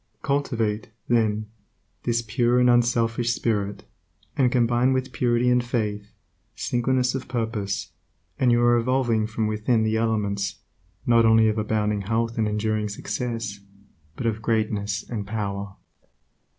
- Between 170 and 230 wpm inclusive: No, slow, 135 wpm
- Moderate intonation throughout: No, narrow, 2.2 semitones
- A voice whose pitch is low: Yes, low, 115 Hz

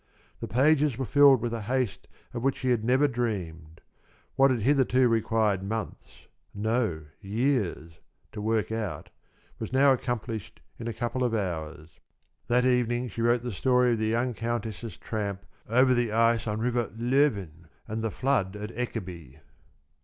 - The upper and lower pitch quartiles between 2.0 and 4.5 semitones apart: Yes, average, 3.2 semitones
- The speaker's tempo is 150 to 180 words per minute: Yes, average, 160 wpm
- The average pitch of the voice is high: No, low, 115 Hz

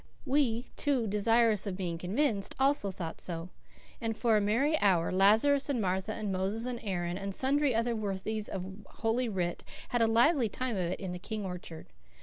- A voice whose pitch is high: Yes, high, 215 Hz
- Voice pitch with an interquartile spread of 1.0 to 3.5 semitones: No, average, 4.1 semitones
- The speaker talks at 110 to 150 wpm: No, average, 185 wpm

